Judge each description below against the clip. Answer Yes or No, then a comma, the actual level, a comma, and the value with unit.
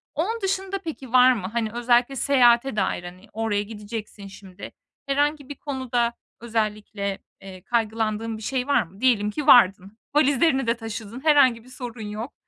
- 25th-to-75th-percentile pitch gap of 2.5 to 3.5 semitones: No, average, 4.2 semitones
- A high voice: Yes, high, 235 Hz